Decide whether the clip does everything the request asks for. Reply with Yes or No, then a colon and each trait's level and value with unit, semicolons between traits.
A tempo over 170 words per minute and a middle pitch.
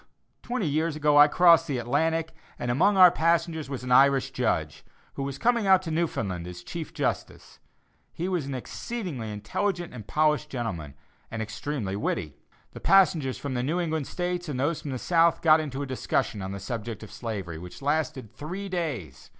Yes: average, 185 wpm; medium, 145 Hz